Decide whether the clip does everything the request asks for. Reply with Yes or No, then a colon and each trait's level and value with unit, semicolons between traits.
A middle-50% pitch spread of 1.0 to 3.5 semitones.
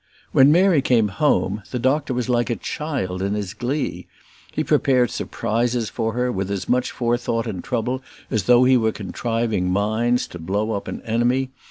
Yes: average, 3.2 semitones